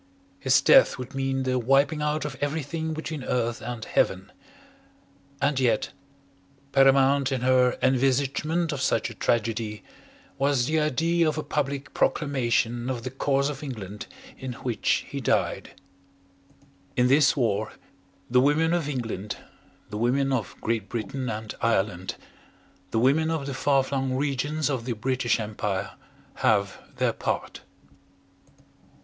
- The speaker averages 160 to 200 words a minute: No, average, 140 wpm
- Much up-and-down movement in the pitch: No, average, 3.4 semitones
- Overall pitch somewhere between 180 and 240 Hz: No, low, 130 Hz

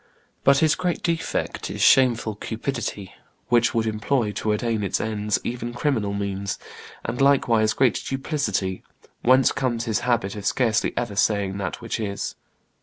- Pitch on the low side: Yes, low, 115 Hz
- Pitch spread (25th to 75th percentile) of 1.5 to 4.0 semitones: Yes, average, 3.7 semitones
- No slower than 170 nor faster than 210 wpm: No, average, 150 wpm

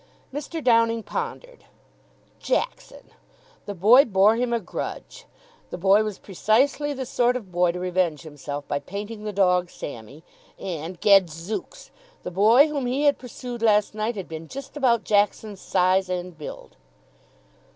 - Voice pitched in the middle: No, high, 210 Hz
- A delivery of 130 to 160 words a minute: Yes, average, 150 wpm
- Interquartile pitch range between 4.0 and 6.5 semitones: Yes, average, 5.3 semitones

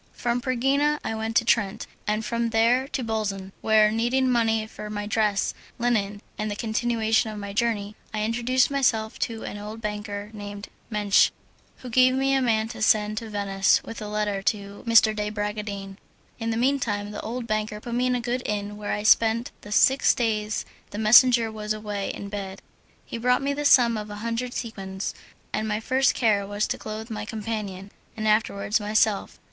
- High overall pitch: Yes, high, 220 Hz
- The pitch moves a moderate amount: No, narrow, 2.1 semitones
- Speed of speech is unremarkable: Yes, average, 195 wpm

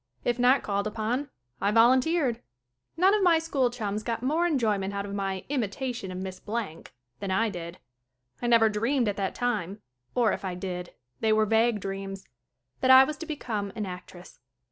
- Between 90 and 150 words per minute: No, average, 185 wpm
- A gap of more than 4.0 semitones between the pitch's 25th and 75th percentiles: Yes, average, 4.5 semitones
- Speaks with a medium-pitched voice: No, high, 220 Hz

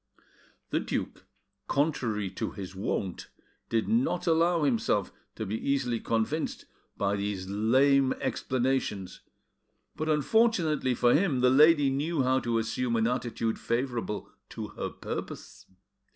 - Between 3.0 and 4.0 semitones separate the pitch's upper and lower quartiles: No, average, 5.0 semitones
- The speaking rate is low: Yes, slow, 125 wpm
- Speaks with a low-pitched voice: Yes, low, 125 Hz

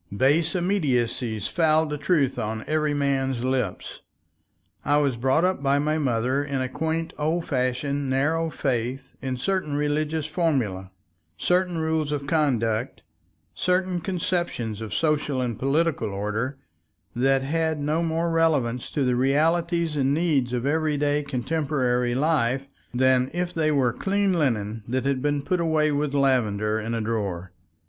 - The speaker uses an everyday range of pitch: Yes, average, 4.1 semitones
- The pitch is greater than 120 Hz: Yes, medium, 140 Hz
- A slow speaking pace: No, average, 145 wpm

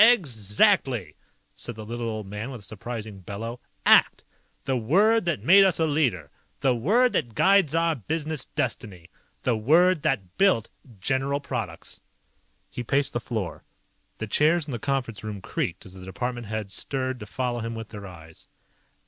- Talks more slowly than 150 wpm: No, average, 165 wpm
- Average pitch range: No, wide, 5.9 semitones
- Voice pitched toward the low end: Yes, low, 120 Hz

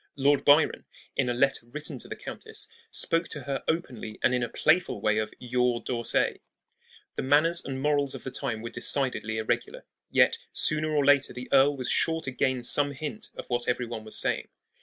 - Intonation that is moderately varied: Yes, average, 3.2 semitones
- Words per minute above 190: Yes, average, 200 wpm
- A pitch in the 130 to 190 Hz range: Yes, low, 135 Hz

